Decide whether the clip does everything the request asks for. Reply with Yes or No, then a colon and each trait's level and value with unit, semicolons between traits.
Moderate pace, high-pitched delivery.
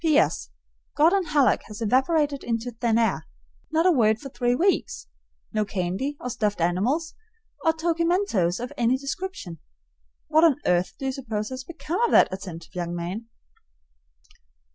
Yes: average, 155 wpm; very high, 250 Hz